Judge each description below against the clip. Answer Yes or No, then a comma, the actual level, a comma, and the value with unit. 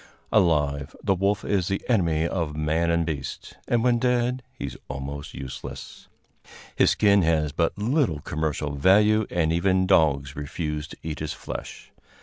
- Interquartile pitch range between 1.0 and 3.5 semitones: No, average, 5.0 semitones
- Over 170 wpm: No, average, 155 wpm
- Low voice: Yes, very low, 85 Hz